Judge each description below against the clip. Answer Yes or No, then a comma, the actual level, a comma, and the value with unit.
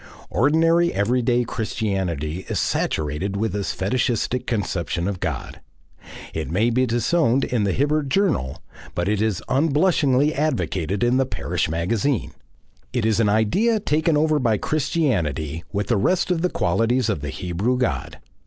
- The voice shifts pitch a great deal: Yes, wide, 6.9 semitones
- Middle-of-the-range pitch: No, low, 115 Hz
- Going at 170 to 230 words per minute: No, average, 150 wpm